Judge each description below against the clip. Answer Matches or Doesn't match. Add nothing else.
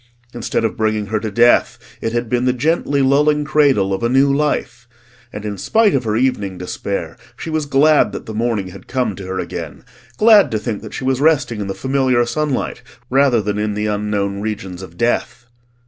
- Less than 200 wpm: Doesn't match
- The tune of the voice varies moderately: Matches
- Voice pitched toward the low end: Matches